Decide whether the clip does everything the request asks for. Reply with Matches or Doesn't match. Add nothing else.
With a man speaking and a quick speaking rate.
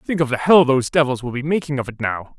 Matches